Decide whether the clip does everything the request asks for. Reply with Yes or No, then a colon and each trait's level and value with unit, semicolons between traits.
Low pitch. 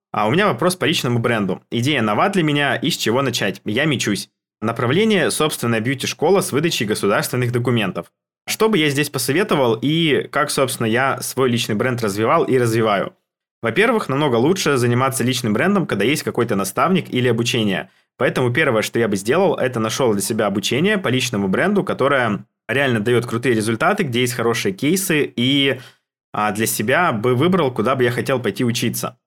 Yes: low, 125 Hz